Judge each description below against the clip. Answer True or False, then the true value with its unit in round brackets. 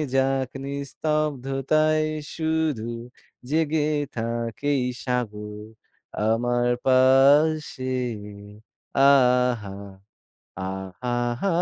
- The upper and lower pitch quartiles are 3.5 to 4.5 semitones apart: True (4.0 semitones)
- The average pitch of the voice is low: True (130 Hz)